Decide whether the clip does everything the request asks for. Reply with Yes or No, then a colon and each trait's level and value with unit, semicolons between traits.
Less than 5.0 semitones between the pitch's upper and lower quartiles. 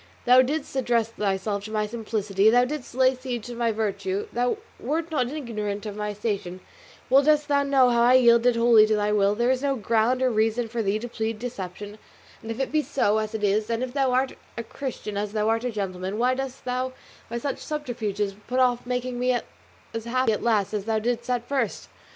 Yes: average, 3.2 semitones